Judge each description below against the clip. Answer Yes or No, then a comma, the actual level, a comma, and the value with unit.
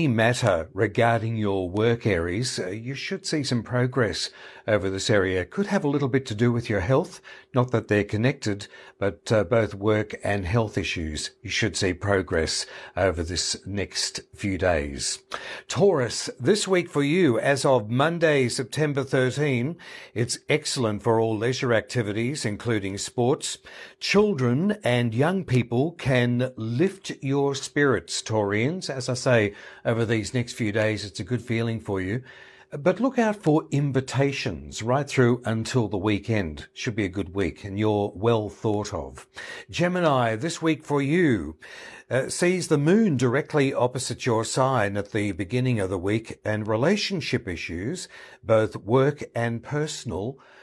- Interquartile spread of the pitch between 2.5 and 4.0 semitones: No, average, 4.8 semitones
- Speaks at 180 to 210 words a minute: No, average, 155 wpm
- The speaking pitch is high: No, low, 120 Hz